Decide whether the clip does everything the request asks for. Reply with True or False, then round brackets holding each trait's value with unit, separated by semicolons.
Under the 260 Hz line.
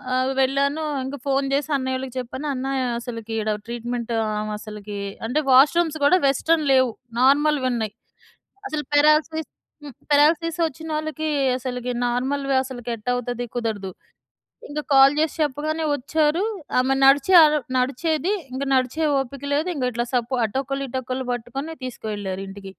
False (265 Hz)